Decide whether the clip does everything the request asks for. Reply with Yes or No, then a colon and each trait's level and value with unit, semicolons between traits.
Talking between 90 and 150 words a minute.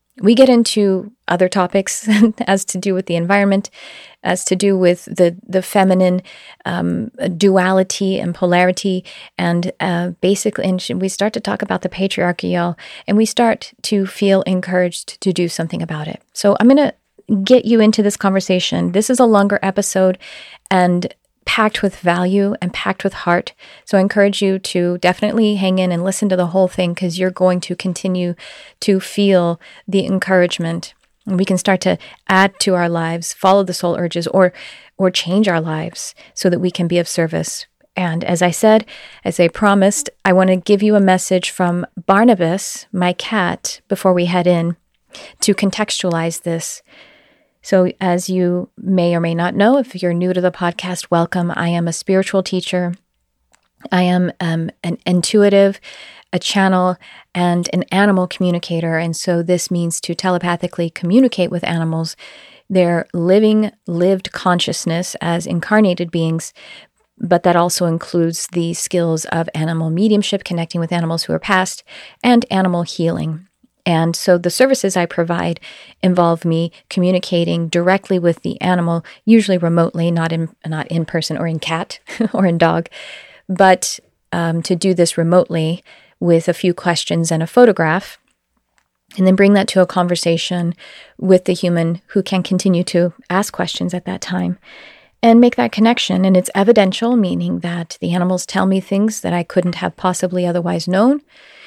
No: average, 165 wpm